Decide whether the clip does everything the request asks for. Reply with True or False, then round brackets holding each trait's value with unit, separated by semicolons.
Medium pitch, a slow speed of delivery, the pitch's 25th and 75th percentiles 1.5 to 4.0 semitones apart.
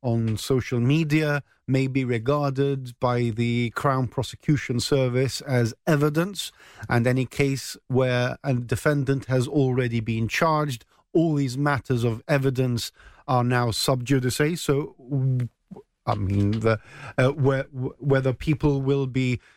False (130 Hz; 125 wpm; 2.6 semitones)